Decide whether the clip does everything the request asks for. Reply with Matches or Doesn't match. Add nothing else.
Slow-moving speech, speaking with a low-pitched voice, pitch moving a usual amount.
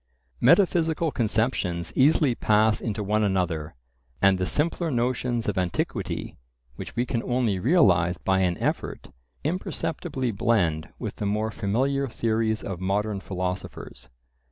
Matches